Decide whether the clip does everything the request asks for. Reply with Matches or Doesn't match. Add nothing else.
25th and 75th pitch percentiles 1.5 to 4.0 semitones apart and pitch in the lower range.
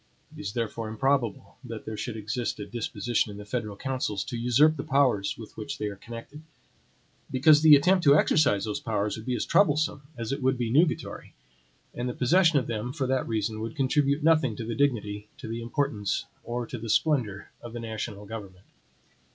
Doesn't match